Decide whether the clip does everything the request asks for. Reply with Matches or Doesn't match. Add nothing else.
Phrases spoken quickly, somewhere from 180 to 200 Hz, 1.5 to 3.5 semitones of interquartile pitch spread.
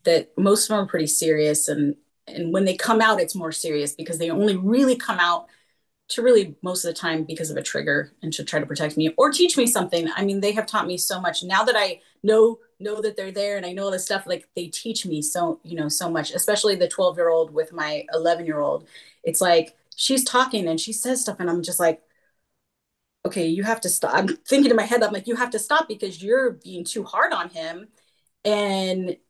Doesn't match